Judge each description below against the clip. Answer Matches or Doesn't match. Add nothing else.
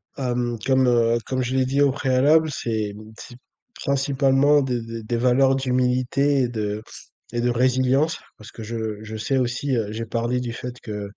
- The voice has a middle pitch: Doesn't match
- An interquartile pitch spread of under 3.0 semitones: Matches